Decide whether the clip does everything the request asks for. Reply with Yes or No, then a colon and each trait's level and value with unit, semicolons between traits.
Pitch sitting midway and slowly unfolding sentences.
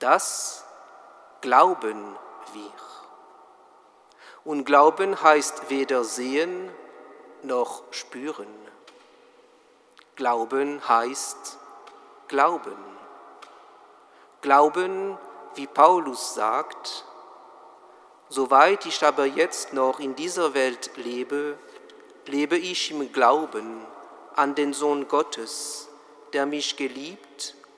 Yes: medium, 150 Hz; slow, 80 wpm